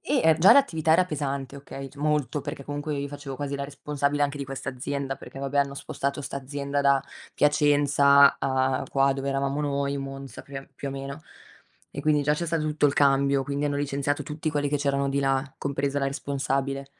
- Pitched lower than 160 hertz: Yes, medium, 140 Hz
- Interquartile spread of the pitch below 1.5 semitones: Yes, narrow, 1.1 semitones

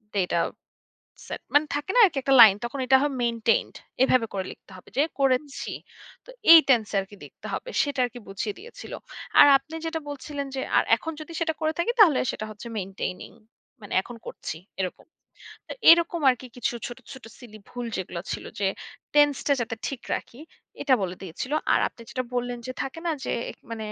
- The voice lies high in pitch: Yes, very high, 255 Hz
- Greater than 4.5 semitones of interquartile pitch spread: Yes, average, 5.0 semitones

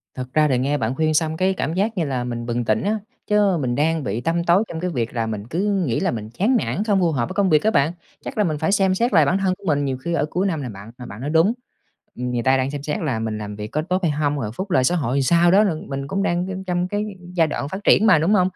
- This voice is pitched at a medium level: Yes, medium, 155 Hz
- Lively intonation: Yes, wide, 6.5 semitones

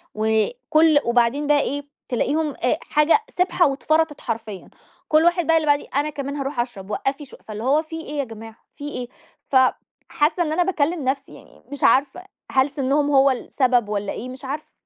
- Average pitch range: Yes, average, 3.6 semitones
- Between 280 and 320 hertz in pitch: Yes, very high, 285 Hz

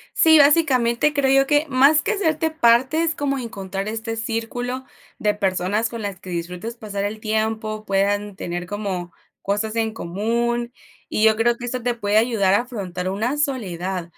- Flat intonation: No, average, 3.9 semitones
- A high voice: Yes, high, 225 Hz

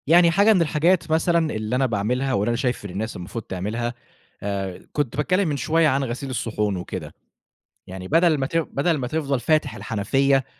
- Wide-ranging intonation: Yes, wide, 6.0 semitones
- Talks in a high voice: No, low, 135 Hz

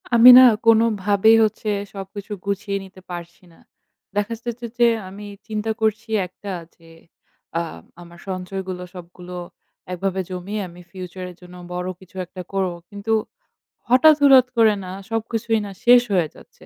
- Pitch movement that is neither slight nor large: Yes, average, 3.6 semitones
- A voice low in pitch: No, high, 200 Hz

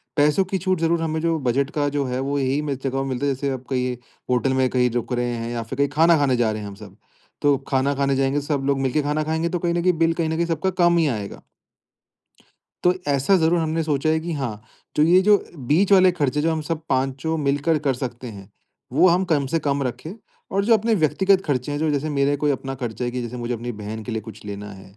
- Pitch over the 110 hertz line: Yes, medium, 140 Hz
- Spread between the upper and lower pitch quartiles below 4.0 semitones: No, average, 4.3 semitones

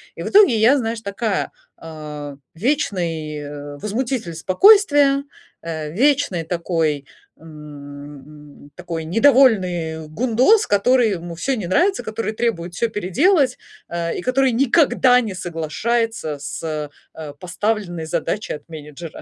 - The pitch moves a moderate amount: No, wide, 7.3 semitones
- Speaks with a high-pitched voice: No, medium, 180 Hz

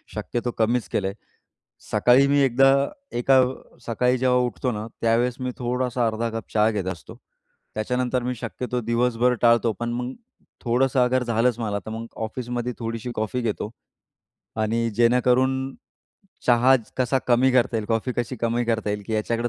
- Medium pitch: No, low, 120 Hz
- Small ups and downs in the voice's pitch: Yes, narrow, 1.8 semitones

